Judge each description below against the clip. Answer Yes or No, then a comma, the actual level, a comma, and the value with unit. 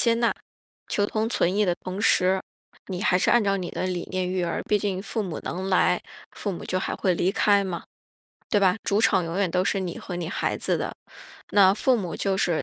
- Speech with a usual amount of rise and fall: No, narrow, 2.0 semitones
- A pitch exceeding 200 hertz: No, high, 190 Hz